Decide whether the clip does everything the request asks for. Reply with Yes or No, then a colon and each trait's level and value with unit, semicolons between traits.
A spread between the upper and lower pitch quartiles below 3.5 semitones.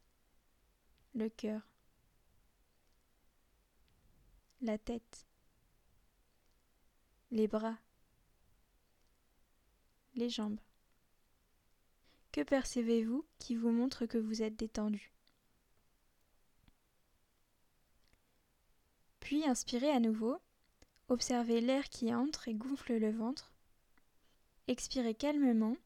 Yes: average, 2.7 semitones